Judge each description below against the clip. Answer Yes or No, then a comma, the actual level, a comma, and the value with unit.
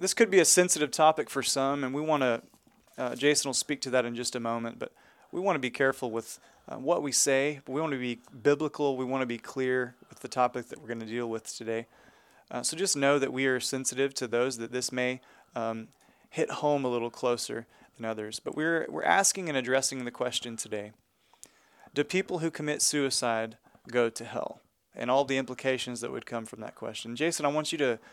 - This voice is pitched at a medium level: No, low, 130 Hz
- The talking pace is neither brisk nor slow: No, fast, 230 wpm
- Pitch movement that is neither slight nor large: Yes, average, 3.3 semitones